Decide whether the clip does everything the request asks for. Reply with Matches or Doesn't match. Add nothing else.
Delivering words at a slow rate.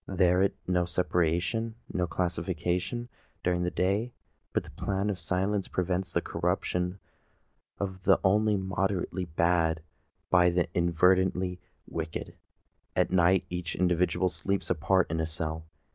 Matches